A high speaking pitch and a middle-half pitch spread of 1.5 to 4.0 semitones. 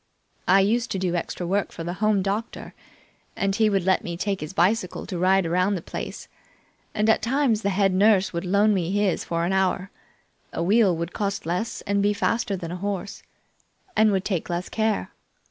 Yes: high, 195 Hz; narrow, 2.6 semitones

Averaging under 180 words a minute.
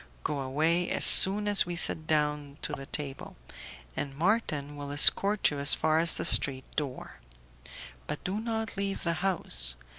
Yes: average, 160 wpm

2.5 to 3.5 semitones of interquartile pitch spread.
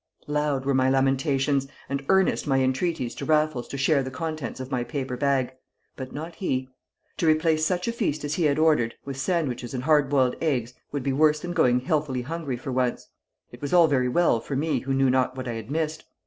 Yes: average, 3.2 semitones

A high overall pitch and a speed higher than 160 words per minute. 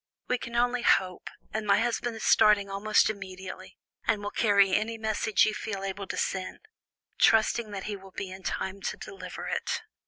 Yes: high, 205 Hz; average, 185 wpm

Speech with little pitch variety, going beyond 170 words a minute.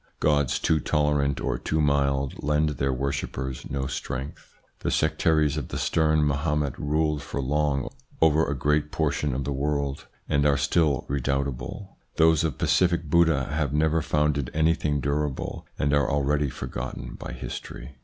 No: narrow, 1.9 semitones; average, 155 wpm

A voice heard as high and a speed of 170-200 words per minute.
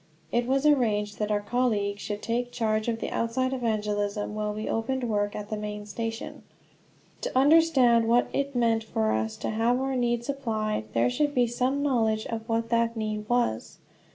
Yes: high, 230 Hz; average, 180 wpm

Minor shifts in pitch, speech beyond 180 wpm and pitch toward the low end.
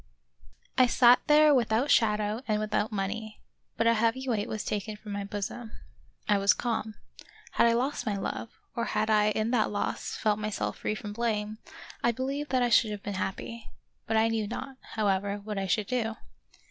No: narrow, 2.1 semitones; average, 190 wpm; high, 220 Hz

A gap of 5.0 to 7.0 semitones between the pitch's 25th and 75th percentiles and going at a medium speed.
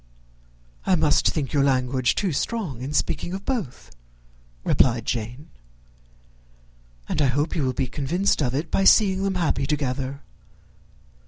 Yes: wide, 5.5 semitones; average, 145 wpm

